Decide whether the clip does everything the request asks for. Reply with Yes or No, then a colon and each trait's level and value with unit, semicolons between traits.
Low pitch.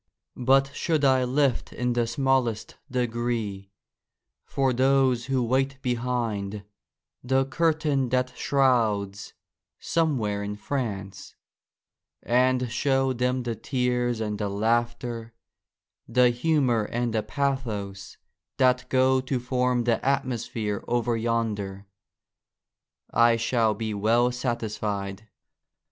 Yes: low, 120 Hz